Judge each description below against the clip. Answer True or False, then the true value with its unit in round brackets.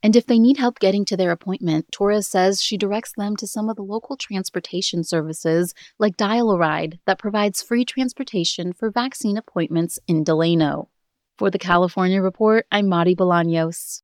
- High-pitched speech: True (195 Hz)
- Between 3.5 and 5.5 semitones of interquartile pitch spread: True (3.9 semitones)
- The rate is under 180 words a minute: True (165 wpm)